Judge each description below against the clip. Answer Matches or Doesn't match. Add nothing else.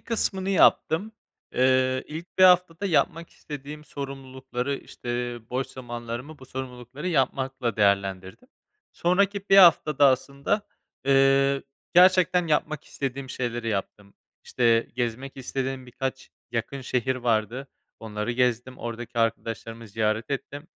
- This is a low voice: Matches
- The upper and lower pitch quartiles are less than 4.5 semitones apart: Matches